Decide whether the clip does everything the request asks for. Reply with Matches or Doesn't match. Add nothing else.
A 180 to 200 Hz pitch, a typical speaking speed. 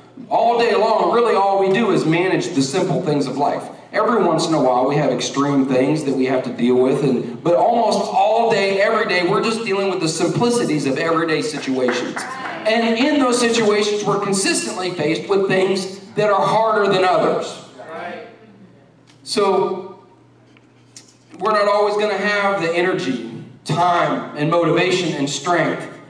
Matches